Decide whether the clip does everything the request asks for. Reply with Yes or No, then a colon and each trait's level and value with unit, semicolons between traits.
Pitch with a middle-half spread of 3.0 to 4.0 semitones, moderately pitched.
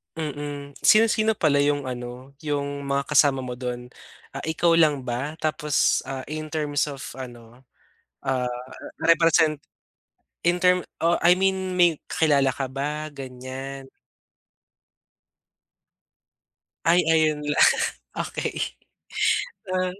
Yes: average, 3.3 semitones; medium, 145 Hz